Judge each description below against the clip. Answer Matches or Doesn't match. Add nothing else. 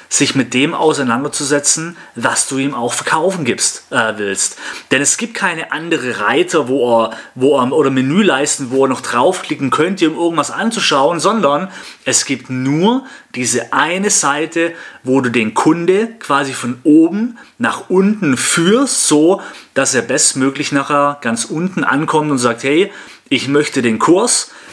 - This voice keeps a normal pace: Matches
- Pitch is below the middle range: Doesn't match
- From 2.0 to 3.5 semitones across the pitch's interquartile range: Doesn't match